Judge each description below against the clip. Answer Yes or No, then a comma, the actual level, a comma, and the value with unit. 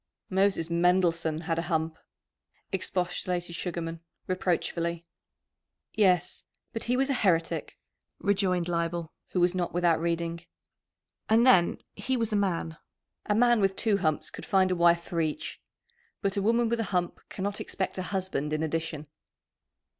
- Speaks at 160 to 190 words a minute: No, average, 150 wpm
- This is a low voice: No, medium, 180 Hz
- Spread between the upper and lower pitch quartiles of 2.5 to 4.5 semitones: Yes, average, 2.9 semitones